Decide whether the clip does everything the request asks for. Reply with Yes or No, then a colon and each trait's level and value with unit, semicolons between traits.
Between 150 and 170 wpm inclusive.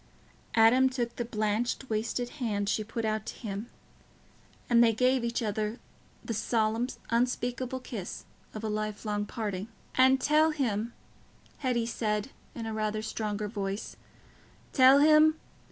No: slow, 135 wpm